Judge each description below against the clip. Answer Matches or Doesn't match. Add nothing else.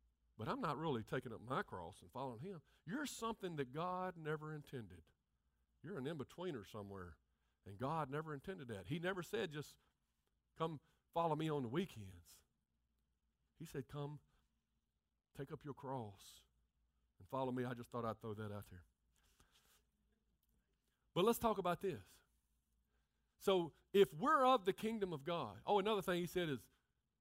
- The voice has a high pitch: Doesn't match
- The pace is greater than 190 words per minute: Doesn't match